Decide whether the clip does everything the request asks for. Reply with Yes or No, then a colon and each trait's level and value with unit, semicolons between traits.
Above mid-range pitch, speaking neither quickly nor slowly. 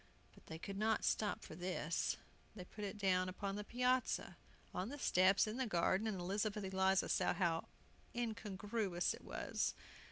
Yes: high, 195 Hz; average, 165 wpm